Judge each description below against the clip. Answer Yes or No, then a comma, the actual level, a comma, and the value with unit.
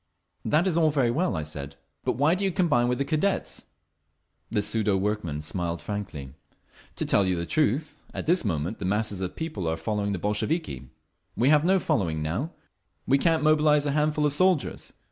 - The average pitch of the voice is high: No, low, 120 Hz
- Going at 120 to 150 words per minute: No, average, 190 wpm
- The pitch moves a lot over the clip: Yes, wide, 8.7 semitones